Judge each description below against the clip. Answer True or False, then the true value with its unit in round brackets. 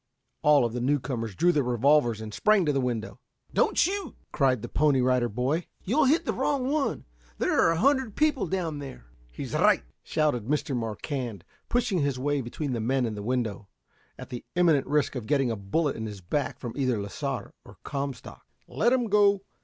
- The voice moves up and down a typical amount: False (5.9 semitones)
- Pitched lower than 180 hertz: True (140 Hz)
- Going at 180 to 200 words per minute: True (195 wpm)